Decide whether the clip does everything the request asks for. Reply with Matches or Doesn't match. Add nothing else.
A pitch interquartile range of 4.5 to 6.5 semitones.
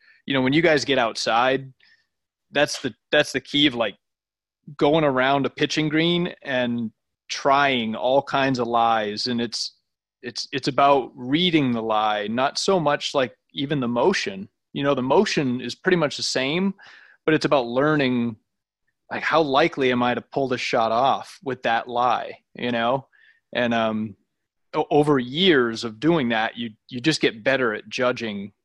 Doesn't match